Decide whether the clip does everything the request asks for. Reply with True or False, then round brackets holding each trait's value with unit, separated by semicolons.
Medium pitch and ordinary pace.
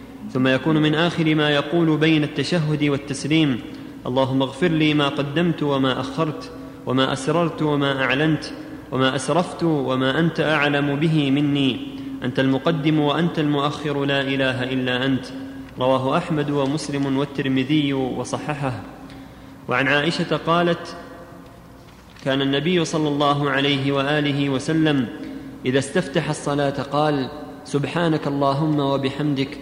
True (145 Hz; 115 wpm)